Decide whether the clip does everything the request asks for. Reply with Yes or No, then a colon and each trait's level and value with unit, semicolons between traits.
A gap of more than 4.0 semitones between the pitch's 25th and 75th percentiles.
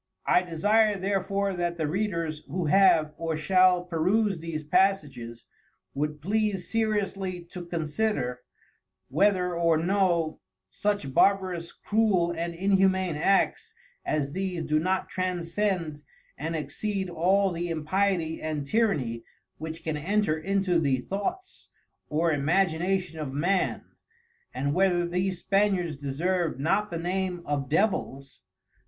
No: average, 3.7 semitones